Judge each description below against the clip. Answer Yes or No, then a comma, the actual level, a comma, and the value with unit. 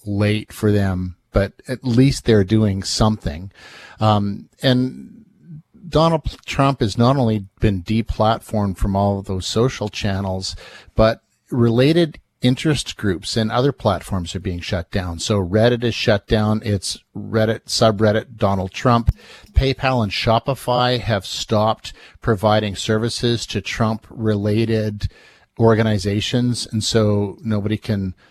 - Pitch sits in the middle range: No, low, 110 Hz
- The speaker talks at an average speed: No, slow, 125 wpm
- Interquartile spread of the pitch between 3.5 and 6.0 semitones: No, average, 2.9 semitones